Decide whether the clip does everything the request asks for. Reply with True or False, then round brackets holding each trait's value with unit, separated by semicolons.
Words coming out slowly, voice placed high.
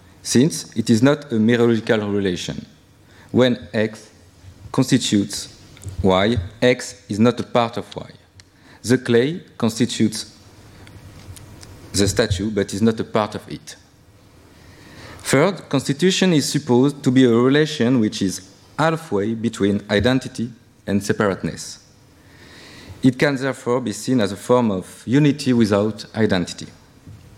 False (125 wpm; 110 Hz)